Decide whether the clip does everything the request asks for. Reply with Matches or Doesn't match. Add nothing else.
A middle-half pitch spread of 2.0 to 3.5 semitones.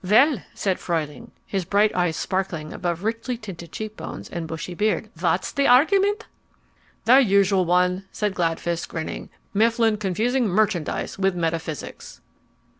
Doesn't match